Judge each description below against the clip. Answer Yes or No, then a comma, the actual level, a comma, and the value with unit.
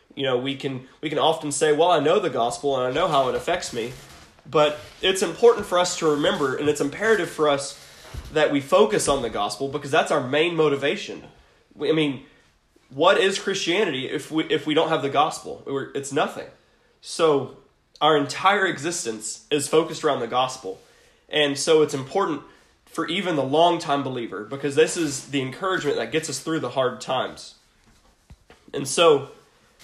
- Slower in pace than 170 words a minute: No, average, 185 wpm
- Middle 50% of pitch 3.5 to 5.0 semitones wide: No, average, 3.0 semitones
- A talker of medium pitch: Yes, medium, 150 Hz